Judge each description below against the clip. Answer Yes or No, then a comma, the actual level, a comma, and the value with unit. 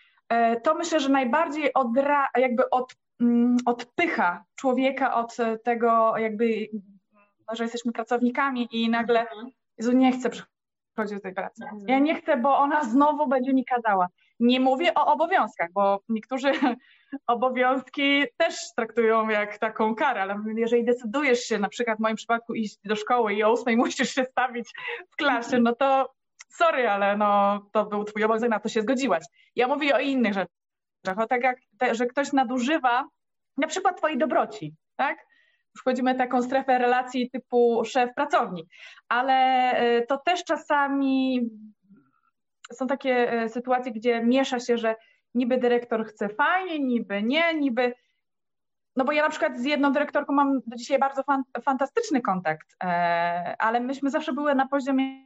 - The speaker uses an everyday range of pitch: Yes, average, 3.5 semitones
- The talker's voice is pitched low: No, very high, 250 Hz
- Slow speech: No, average, 150 wpm